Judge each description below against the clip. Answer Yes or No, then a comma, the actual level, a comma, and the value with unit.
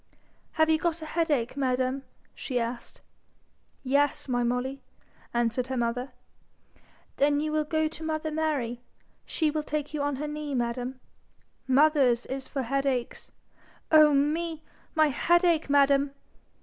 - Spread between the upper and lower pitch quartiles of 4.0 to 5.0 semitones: No, average, 3.4 semitones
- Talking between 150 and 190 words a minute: No, slow, 135 wpm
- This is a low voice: No, very high, 280 Hz